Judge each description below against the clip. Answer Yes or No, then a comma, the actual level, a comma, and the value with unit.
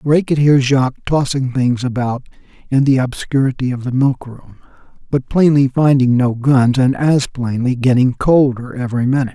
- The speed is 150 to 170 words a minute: Yes, average, 165 wpm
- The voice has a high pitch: No, low, 130 Hz